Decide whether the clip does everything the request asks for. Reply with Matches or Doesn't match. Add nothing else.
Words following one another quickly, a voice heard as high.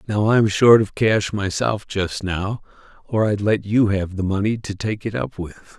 Doesn't match